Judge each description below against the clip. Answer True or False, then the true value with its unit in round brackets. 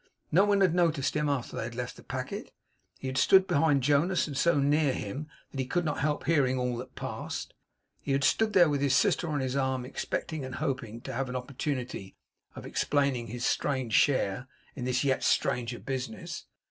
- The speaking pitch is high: False (135 Hz)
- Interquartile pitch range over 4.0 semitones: False (3.1 semitones)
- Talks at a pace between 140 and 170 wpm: False (200 wpm)